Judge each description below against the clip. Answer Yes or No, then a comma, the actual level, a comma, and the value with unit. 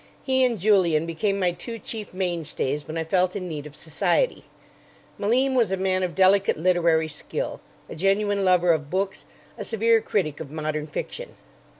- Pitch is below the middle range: No, medium, 185 Hz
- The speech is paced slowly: No, average, 175 wpm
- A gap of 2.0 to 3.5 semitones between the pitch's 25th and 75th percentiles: No, average, 4.1 semitones